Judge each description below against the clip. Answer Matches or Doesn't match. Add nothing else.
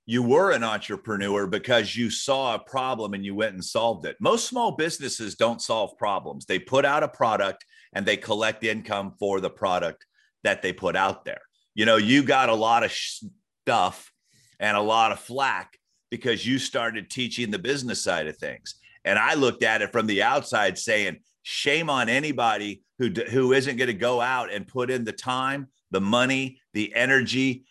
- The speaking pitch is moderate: Doesn't match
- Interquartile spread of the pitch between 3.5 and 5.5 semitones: Matches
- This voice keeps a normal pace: Matches